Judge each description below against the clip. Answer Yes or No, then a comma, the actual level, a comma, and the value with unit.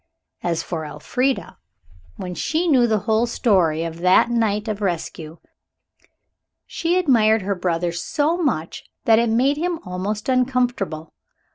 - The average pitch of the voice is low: No, high, 220 Hz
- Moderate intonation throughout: No, wide, 6.2 semitones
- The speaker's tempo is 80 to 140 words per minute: Yes, slow, 135 wpm